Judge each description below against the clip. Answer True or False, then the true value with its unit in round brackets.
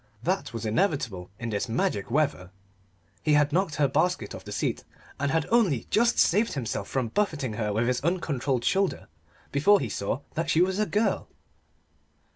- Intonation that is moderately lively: False (7.8 semitones)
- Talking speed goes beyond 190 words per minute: False (175 wpm)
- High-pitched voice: False (145 Hz)